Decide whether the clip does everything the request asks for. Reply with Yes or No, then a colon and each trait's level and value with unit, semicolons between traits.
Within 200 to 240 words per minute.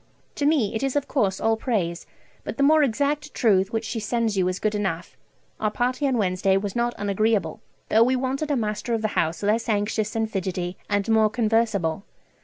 Yes: fast, 205 wpm